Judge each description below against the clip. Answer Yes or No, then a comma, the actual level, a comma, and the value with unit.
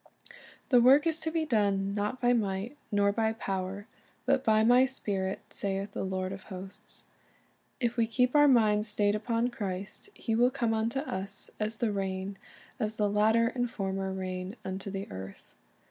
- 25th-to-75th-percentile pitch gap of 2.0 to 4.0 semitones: Yes, average, 3.7 semitones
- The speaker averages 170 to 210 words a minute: Yes, average, 175 wpm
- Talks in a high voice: Yes, high, 210 Hz